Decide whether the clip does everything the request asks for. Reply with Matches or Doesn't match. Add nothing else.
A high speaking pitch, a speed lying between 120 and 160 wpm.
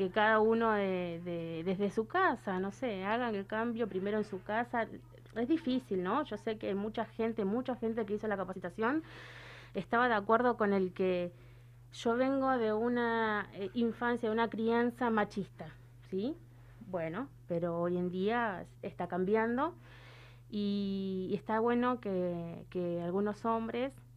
Matches